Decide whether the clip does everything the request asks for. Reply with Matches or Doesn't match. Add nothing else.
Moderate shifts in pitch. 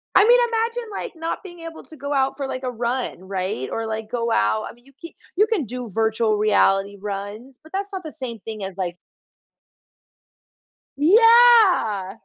Doesn't match